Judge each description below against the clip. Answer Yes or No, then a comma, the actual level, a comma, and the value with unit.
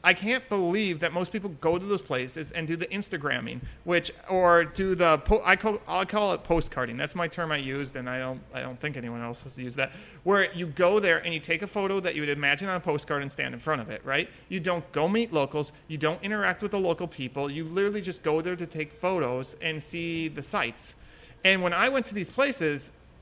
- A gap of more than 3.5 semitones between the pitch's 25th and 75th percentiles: Yes, average, 4.4 semitones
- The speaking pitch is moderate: Yes, medium, 170 Hz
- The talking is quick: Yes, fast, 245 wpm